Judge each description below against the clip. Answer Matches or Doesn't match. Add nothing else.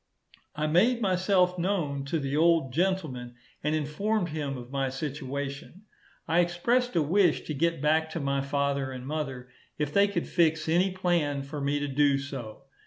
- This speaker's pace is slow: Doesn't match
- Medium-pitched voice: Matches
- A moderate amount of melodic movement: Matches